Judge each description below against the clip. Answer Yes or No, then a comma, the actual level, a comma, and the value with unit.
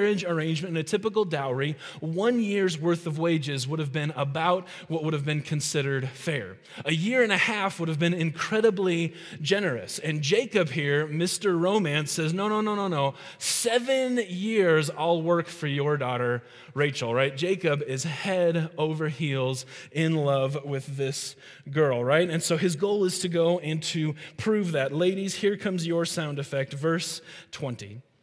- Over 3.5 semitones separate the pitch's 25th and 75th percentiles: Yes, average, 3.9 semitones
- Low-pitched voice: No, medium, 165 Hz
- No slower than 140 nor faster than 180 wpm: Yes, average, 170 wpm